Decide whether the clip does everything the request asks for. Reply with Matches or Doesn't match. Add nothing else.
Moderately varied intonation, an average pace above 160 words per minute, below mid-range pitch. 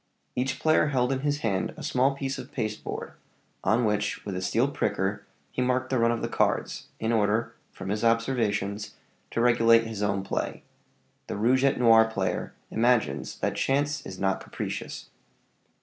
Matches